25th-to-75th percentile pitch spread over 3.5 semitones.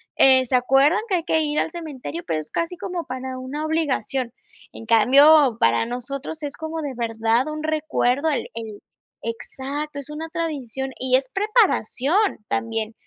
Yes: average, 4.2 semitones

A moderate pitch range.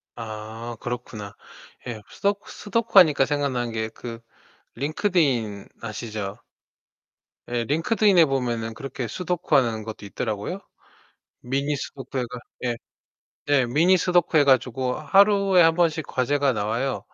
No: wide, 6.0 semitones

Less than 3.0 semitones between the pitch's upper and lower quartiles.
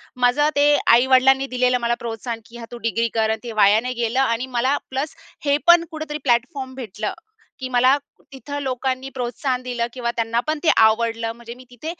Yes: narrow, 2.5 semitones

